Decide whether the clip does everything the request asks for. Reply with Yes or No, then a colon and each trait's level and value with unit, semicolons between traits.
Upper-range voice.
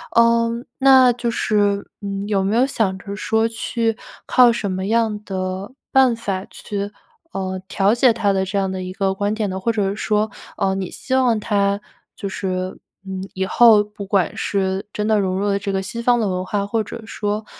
Yes: high, 205 Hz